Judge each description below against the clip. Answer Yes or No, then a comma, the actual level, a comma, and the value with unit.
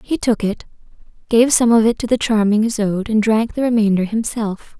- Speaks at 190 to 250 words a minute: Yes, average, 200 wpm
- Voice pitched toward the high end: Yes, high, 220 Hz